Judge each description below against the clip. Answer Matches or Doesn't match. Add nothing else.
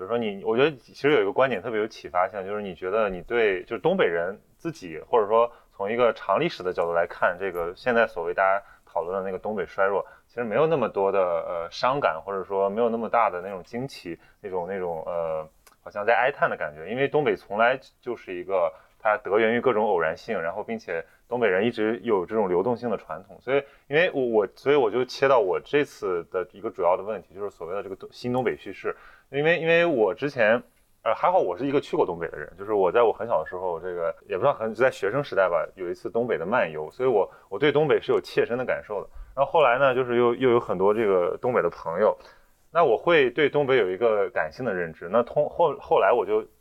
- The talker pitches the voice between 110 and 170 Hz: Doesn't match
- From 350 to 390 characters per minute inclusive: Matches